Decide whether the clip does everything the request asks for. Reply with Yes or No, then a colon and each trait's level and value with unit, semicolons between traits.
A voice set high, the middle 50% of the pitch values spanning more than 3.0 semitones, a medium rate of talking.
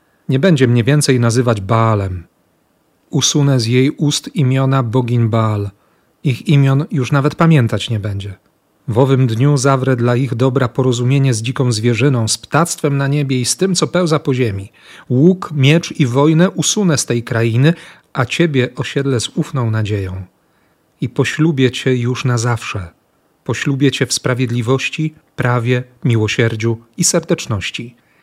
No: low, 130 Hz; average, 3.5 semitones; average, 150 wpm